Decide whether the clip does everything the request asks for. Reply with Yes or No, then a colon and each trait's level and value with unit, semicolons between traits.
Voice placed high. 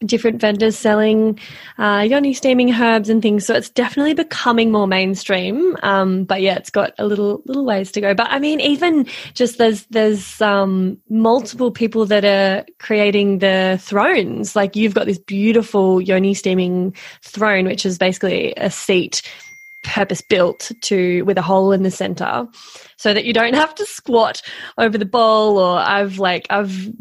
Yes: high, 210 Hz